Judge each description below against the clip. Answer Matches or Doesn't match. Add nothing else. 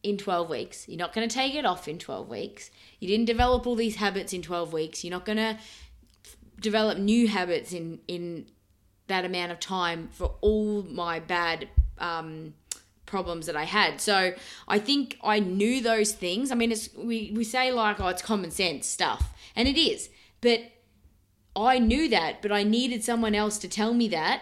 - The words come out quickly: Doesn't match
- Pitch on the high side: Matches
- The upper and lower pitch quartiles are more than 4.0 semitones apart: Matches